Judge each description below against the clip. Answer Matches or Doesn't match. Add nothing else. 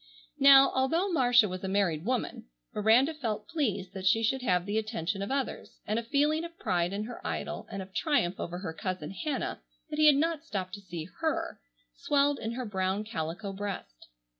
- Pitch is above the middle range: Matches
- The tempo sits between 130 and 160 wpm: Doesn't match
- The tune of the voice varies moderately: Doesn't match